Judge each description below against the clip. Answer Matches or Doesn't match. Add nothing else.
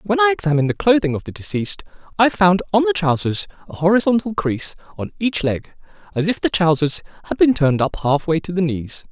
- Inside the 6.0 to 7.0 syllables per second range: Matches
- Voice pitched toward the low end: Doesn't match